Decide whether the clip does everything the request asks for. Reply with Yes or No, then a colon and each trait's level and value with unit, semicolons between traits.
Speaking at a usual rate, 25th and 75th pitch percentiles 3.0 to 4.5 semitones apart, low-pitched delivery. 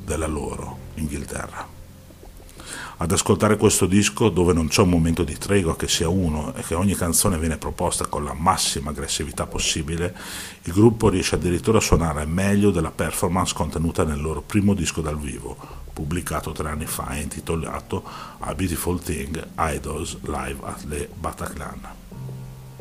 Yes: average, 155 wpm; average, 3.6 semitones; very low, 85 Hz